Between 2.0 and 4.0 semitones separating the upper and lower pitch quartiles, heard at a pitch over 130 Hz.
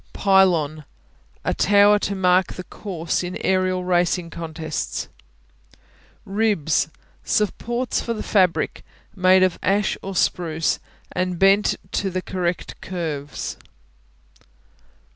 Yes: narrow, 2.4 semitones; medium, 185 Hz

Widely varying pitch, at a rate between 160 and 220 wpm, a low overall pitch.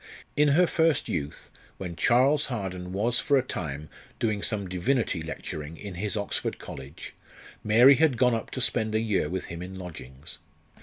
Yes: wide, 5.9 semitones; average, 170 wpm; low, 105 Hz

